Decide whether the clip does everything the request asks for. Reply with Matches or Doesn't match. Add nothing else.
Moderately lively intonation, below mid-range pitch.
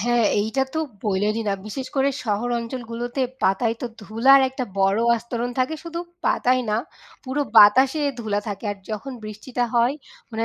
Doesn't match